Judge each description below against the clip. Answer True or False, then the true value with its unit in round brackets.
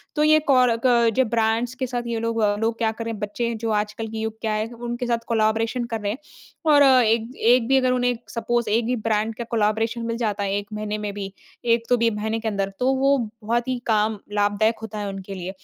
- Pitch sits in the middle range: False (225 Hz)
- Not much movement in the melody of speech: True (2.0 semitones)